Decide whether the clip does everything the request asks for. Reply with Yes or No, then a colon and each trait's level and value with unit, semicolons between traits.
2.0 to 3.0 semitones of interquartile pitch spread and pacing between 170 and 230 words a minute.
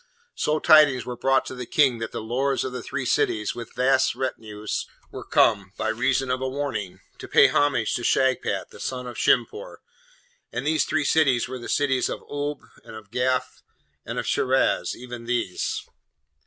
Yes: average, 2.7 semitones; average, 180 wpm